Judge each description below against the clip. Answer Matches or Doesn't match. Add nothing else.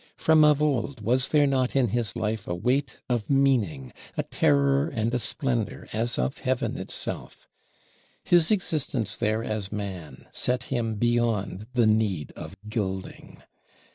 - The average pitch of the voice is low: Matches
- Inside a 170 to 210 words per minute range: Doesn't match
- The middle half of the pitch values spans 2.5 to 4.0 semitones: Doesn't match